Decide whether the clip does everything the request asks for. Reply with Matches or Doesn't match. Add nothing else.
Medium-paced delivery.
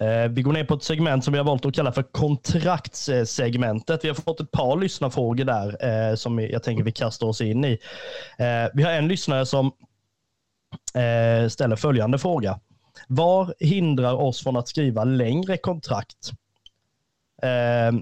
Matches